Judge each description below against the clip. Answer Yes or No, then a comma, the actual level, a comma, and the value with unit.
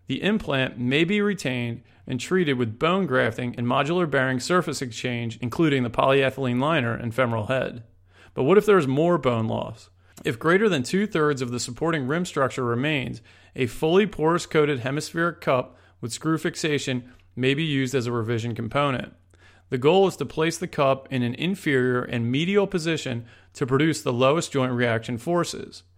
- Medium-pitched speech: No, low, 130 Hz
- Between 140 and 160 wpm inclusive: No, average, 180 wpm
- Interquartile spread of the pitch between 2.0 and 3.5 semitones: No, average, 4.9 semitones